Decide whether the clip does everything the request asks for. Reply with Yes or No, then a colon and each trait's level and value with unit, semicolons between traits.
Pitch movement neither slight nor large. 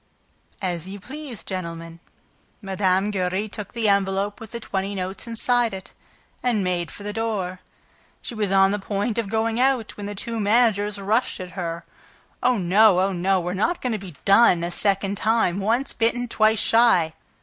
Yes: average, 3.2 semitones